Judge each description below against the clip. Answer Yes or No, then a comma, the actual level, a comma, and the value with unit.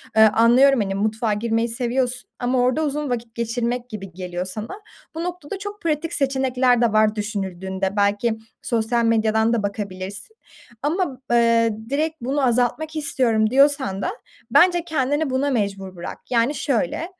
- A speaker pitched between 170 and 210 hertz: No, high, 235 Hz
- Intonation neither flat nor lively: Yes, average, 4.4 semitones